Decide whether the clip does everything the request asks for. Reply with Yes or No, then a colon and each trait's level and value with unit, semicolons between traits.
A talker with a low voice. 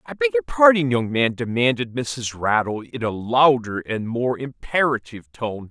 Yes: low, 130 Hz